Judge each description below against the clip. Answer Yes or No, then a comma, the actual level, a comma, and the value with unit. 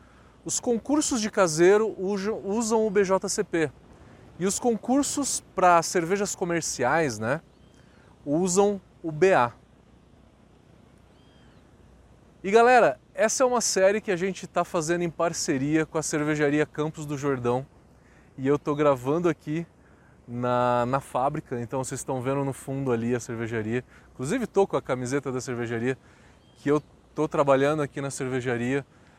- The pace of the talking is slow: No, average, 140 wpm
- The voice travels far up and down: Yes, wide, 6.6 semitones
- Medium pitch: Yes, medium, 155 Hz